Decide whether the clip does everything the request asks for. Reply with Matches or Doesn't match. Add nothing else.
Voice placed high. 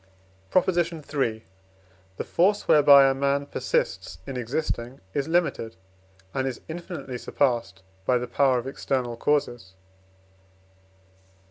Doesn't match